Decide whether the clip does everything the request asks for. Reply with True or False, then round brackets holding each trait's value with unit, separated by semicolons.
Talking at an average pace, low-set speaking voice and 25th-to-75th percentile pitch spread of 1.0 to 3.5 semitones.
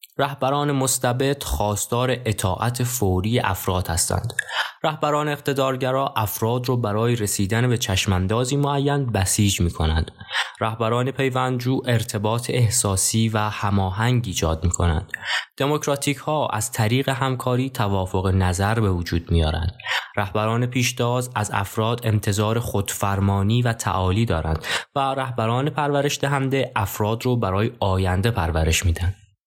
False (120 wpm; 110 Hz; 4.5 semitones)